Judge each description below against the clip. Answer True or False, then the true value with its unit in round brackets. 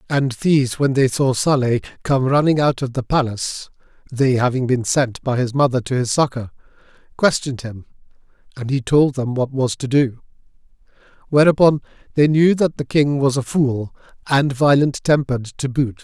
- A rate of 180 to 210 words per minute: False (170 wpm)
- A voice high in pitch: False (135 Hz)